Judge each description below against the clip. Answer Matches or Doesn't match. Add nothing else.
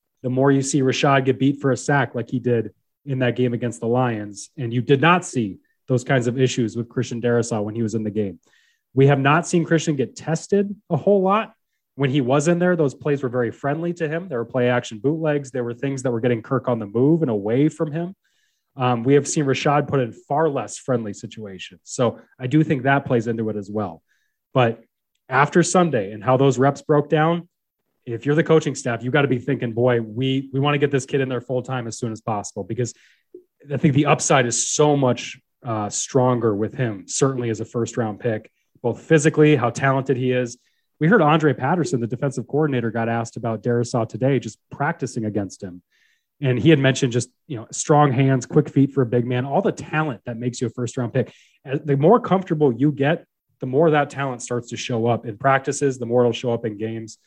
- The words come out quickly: Matches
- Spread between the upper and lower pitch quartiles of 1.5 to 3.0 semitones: Doesn't match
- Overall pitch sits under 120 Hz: Doesn't match